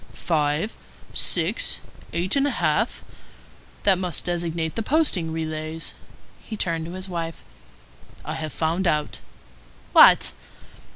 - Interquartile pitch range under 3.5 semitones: Yes, average, 2.7 semitones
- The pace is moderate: No, slow, 120 wpm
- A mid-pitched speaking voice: Yes, medium, 170 Hz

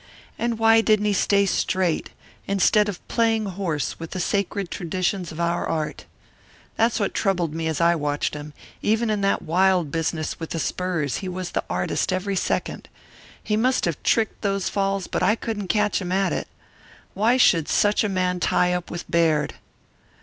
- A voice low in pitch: No, medium, 185 Hz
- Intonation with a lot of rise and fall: No, average, 3.6 semitones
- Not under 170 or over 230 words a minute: Yes, average, 180 wpm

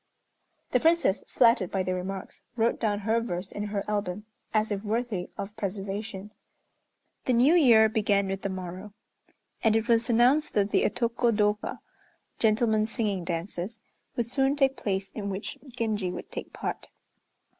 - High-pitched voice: Yes, high, 210 Hz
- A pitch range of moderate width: Yes, average, 3.0 semitones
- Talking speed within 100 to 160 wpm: Yes, average, 155 wpm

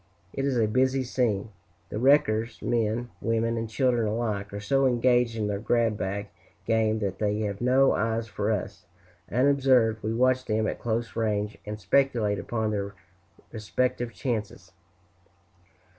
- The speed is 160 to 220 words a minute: No, average, 150 wpm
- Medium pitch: No, low, 115 Hz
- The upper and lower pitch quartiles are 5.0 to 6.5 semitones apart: No, average, 2.7 semitones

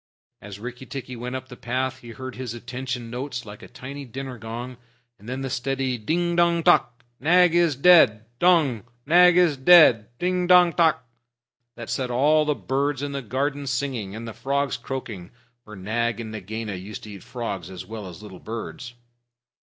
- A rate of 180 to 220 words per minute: Yes, average, 185 wpm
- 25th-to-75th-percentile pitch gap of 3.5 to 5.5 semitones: Yes, average, 4.0 semitones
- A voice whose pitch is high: No, low, 125 Hz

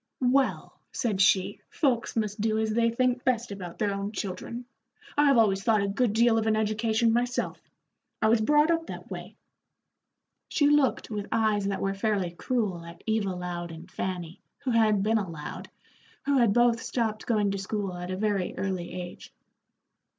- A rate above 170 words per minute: Yes, average, 180 wpm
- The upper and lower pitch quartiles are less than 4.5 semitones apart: Yes, average, 3.3 semitones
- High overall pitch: Yes, high, 215 Hz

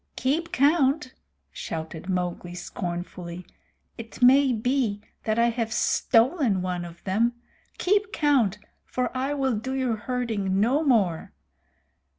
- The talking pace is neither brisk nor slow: No, slow, 125 wpm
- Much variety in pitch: Yes, wide, 6.1 semitones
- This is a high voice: Yes, high, 235 Hz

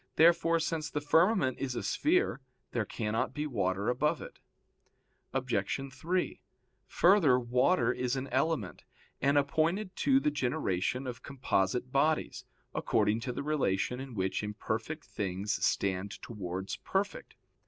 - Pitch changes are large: Yes, wide, 6.2 semitones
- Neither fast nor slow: No, slow, 130 wpm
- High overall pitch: No, low, 130 Hz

